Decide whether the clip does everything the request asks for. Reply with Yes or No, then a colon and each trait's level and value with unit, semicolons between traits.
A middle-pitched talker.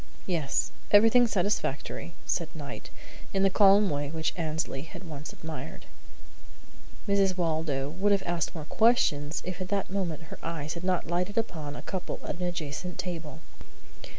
Yes: medium, 170 Hz